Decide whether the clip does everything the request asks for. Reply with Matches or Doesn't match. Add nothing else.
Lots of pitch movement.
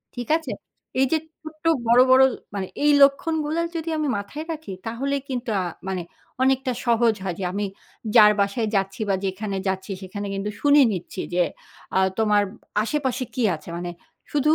Matches